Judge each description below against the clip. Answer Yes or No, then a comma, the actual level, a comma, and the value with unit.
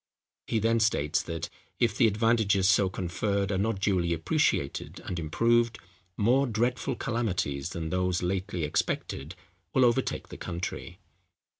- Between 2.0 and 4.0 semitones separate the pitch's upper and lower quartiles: No, average, 4.8 semitones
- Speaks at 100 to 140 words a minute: Yes, slow, 135 wpm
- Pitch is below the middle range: Yes, low, 100 Hz